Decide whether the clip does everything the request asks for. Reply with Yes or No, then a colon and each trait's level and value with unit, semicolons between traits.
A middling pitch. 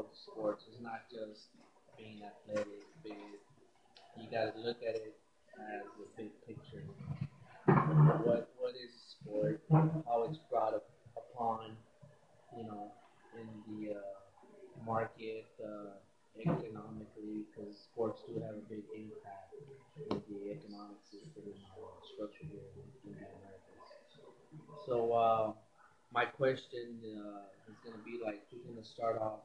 No: low, 110 Hz